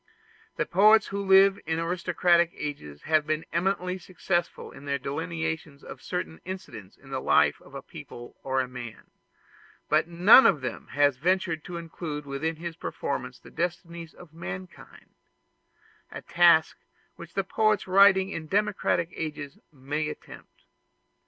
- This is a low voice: No, medium, 165 Hz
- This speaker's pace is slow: No, average, 145 wpm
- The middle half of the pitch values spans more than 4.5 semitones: No, average, 4.1 semitones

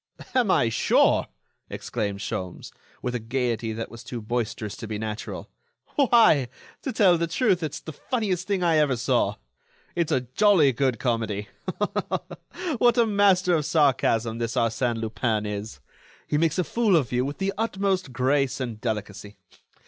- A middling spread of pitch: No, wide, 8.1 semitones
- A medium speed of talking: Yes, average, 160 wpm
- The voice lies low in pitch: Yes, low, 130 Hz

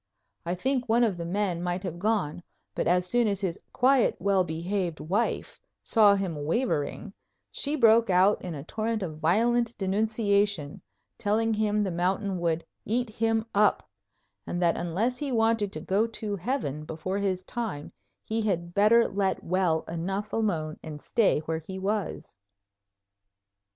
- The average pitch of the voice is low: No, high, 200 Hz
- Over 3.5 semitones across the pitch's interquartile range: Yes, average, 4.3 semitones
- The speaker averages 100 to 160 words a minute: Yes, average, 155 wpm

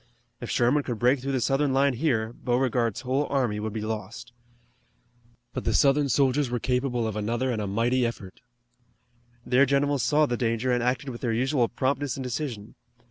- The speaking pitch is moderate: No, low, 125 Hz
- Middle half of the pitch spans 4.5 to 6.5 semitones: No, average, 2.8 semitones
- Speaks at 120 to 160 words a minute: No, average, 185 wpm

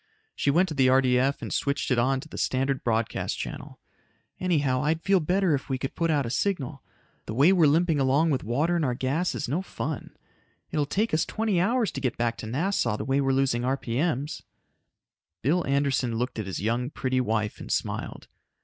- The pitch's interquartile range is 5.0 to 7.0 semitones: No, average, 4.3 semitones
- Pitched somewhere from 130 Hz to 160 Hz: Yes, medium, 140 Hz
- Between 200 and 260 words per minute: Yes, fast, 205 wpm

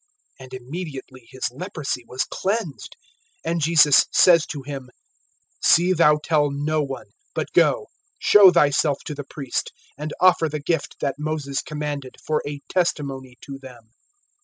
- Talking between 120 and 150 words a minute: Yes, average, 145 wpm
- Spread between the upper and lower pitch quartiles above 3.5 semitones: No, average, 3.0 semitones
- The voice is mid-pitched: Yes, medium, 145 Hz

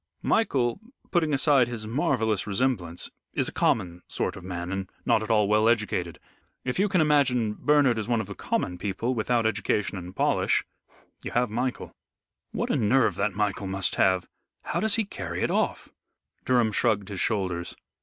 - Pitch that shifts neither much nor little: Yes, average, 4.5 semitones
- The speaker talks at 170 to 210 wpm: Yes, average, 175 wpm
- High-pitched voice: No, low, 110 Hz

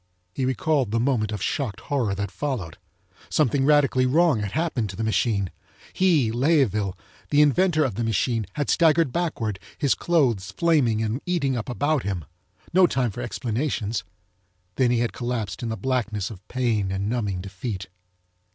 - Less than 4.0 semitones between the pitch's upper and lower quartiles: No, wide, 5.4 semitones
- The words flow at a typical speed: Yes, average, 165 wpm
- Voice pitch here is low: Yes, low, 120 Hz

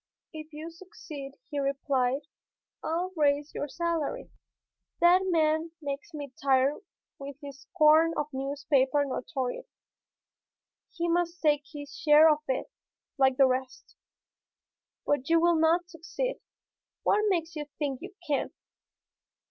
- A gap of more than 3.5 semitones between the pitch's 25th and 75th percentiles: No, average, 3.2 semitones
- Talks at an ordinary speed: No, slow, 125 wpm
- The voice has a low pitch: No, very high, 300 Hz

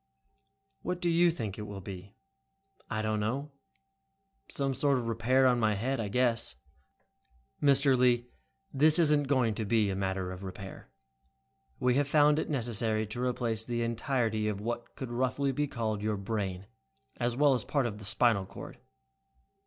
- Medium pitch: No, low, 120 Hz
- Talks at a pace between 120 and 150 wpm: No, average, 170 wpm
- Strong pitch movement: No, average, 4.0 semitones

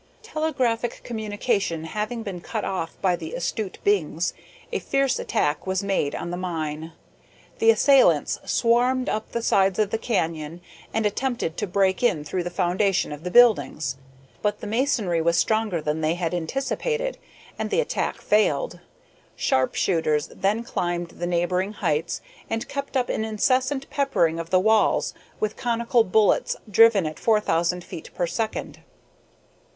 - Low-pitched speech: No, high, 200 Hz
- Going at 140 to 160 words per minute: Yes, average, 155 wpm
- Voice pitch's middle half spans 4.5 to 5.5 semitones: Yes, average, 5.2 semitones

